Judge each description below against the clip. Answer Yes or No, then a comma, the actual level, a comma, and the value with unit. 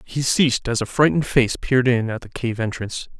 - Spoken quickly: Yes, fast, 225 wpm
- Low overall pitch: Yes, low, 120 Hz